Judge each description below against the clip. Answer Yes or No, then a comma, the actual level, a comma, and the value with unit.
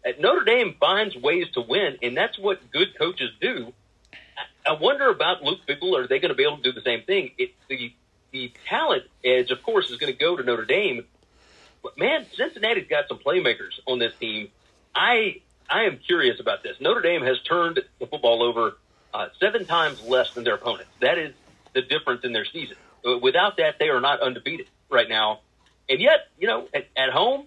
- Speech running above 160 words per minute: Yes, fast, 205 wpm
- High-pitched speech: Yes, very high, 310 Hz